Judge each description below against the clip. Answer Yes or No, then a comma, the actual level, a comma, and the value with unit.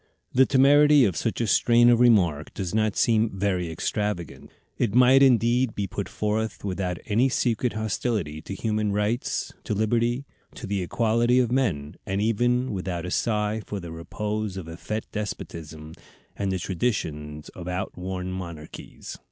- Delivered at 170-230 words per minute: No, average, 155 wpm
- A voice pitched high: No, low, 105 Hz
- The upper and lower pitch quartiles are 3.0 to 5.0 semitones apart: Yes, average, 4.5 semitones